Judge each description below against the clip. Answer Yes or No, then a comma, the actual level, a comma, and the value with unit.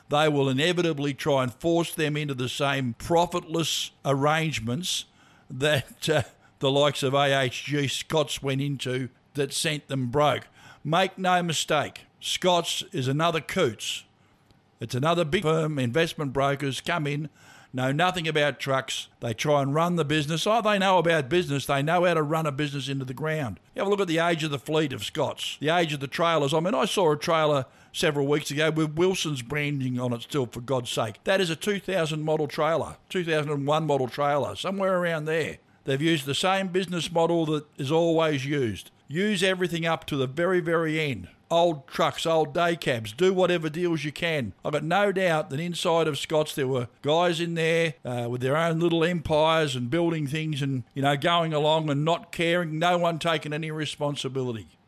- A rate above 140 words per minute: Yes, average, 190 wpm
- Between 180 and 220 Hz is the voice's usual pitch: No, medium, 155 Hz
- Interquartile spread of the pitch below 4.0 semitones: Yes, average, 3.5 semitones